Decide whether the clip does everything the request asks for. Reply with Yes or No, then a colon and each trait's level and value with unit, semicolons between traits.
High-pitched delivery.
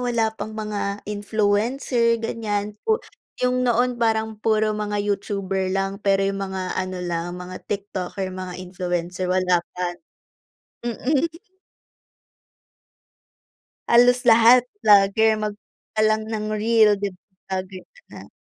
Yes: high, 210 Hz